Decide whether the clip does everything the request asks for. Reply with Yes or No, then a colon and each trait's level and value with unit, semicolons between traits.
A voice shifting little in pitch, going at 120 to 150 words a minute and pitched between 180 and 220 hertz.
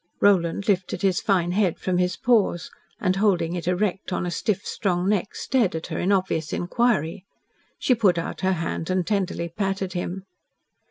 No: narrow, 2.2 semitones; average, 175 wpm; medium, 185 Hz